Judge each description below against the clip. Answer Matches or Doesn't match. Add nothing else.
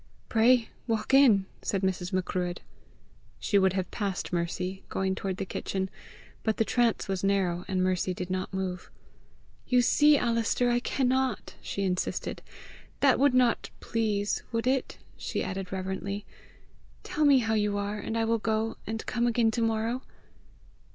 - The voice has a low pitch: Doesn't match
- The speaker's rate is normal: Matches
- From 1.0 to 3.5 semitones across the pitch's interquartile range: Doesn't match